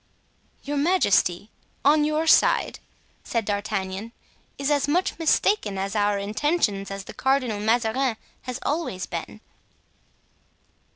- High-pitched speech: Yes, high, 230 Hz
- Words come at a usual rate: No, slow, 120 wpm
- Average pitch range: No, wide, 6.4 semitones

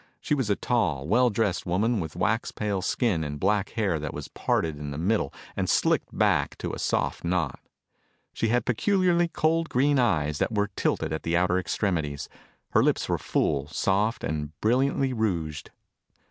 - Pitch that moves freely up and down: Yes, wide, 6.9 semitones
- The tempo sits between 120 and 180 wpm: Yes, average, 175 wpm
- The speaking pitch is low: Yes, low, 100 Hz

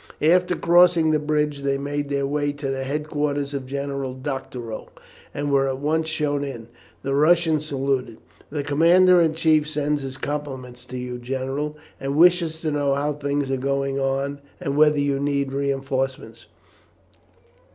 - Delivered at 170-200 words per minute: No, average, 160 wpm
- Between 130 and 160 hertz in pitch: Yes, medium, 140 Hz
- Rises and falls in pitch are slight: Yes, narrow, 1.9 semitones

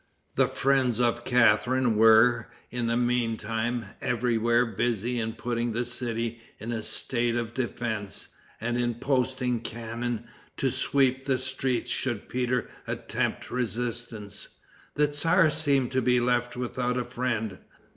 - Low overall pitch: Yes, low, 120 Hz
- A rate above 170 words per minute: No, slow, 135 wpm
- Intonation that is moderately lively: No, narrow, 1.6 semitones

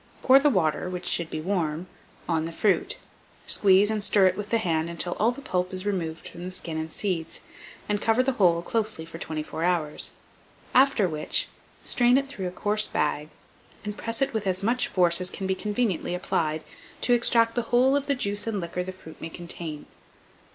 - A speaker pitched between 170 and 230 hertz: Yes, medium, 185 Hz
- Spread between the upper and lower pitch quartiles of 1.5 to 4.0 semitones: No, average, 4.8 semitones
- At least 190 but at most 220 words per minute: Yes, average, 200 wpm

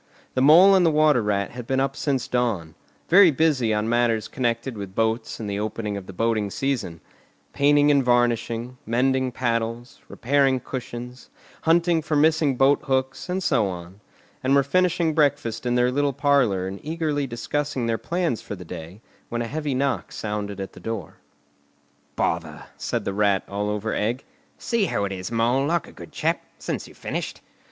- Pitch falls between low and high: No, low, 125 Hz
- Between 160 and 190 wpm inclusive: Yes, average, 180 wpm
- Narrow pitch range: No, average, 5.1 semitones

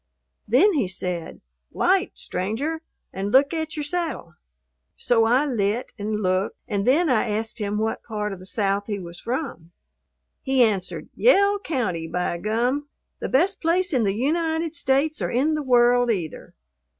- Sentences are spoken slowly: No, average, 160 wpm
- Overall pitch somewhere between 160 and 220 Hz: No, high, 240 Hz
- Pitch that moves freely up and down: Yes, wide, 6.8 semitones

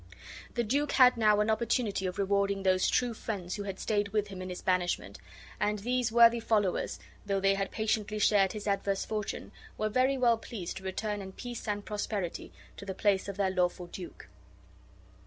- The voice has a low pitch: No, high, 205 Hz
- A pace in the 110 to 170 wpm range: No, average, 190 wpm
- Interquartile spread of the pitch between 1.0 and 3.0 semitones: Yes, narrow, 2.4 semitones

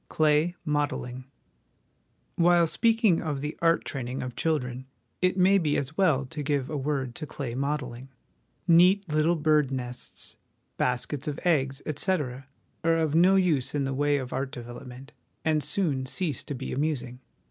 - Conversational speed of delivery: Yes, average, 170 wpm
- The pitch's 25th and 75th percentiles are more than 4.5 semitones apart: No, average, 3.8 semitones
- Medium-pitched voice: Yes, medium, 145 Hz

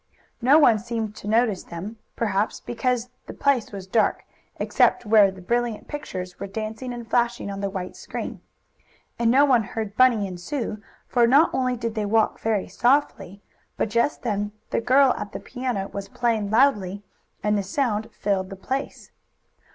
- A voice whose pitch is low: No, high, 220 Hz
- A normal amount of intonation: Yes, average, 3.4 semitones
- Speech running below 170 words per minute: No, average, 175 wpm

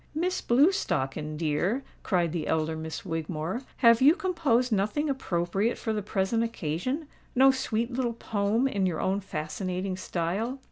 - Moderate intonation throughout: No, wide, 6.9 semitones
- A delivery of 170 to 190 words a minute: No, average, 140 wpm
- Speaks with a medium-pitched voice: No, high, 205 Hz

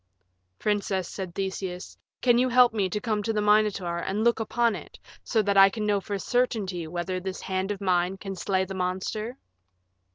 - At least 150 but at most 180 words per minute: No, average, 190 wpm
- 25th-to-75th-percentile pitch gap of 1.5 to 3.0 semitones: Yes, narrow, 2.4 semitones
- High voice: Yes, high, 195 Hz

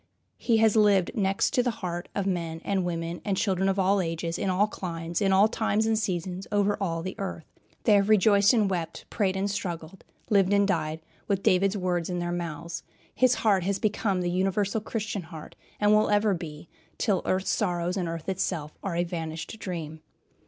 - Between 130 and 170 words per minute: No, average, 195 wpm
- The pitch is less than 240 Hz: Yes, high, 190 Hz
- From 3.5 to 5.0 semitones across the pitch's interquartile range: No, average, 2.9 semitones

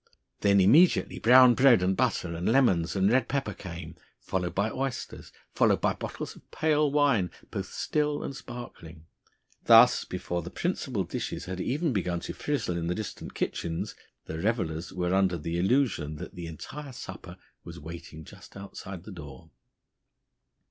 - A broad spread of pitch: Yes, wide, 6.9 semitones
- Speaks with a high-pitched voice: No, very low, 95 Hz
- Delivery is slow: No, average, 160 wpm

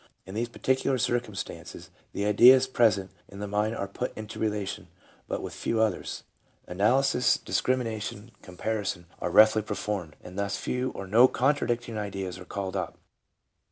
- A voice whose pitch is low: Yes, low, 105 Hz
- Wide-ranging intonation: No, average, 3.5 semitones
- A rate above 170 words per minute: No, average, 155 wpm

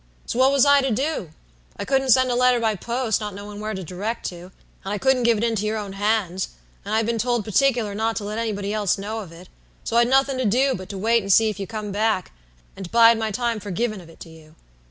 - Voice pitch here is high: Yes, high, 220 Hz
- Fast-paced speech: Yes, fast, 260 wpm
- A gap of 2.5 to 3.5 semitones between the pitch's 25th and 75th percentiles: Yes, average, 3.1 semitones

